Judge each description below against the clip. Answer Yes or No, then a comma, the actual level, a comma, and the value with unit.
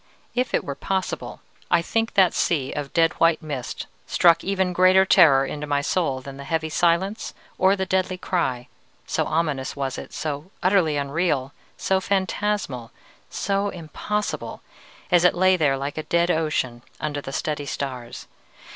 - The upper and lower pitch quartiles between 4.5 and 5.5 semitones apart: Yes, average, 4.9 semitones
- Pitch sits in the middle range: Yes, medium, 165 Hz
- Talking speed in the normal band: Yes, average, 160 wpm